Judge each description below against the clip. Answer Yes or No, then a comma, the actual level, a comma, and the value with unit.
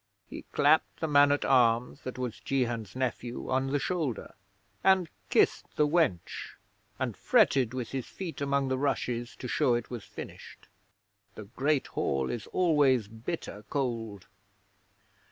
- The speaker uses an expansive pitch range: No, average, 3.5 semitones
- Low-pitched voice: Yes, low, 130 Hz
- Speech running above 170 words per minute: No, average, 145 wpm